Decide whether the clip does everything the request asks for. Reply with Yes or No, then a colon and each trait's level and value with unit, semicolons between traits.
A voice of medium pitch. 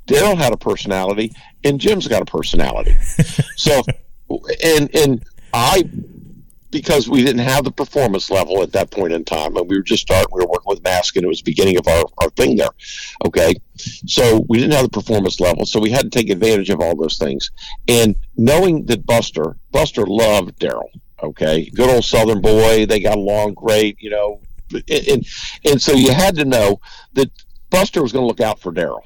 No: low, 115 Hz